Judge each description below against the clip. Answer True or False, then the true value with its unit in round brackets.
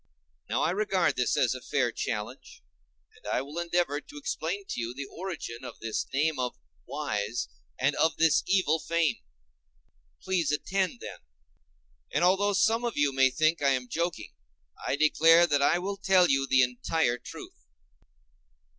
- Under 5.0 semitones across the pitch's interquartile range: False (5.3 semitones)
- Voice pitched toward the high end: False (155 Hz)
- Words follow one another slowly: False (165 wpm)